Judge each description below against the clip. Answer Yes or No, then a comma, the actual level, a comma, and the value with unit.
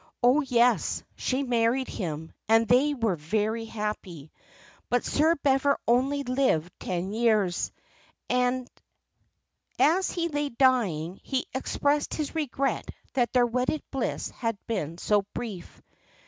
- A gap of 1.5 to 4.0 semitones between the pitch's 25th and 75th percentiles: No, average, 4.4 semitones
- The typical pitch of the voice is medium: No, high, 245 Hz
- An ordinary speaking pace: No, slow, 120 wpm